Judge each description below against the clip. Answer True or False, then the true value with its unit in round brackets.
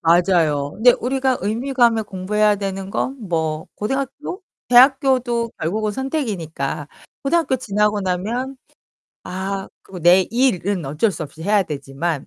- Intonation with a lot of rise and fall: True (6.2 semitones)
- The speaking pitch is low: False (205 Hz)